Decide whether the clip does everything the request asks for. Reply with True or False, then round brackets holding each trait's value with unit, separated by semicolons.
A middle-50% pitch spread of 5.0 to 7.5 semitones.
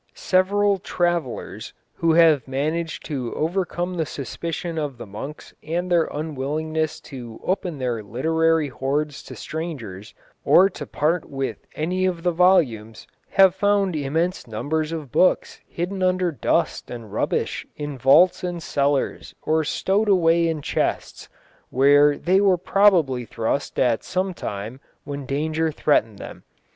False (4.6 semitones)